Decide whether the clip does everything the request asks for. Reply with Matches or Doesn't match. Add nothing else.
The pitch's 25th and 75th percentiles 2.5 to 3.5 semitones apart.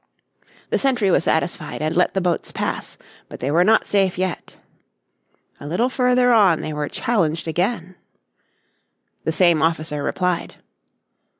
Doesn't match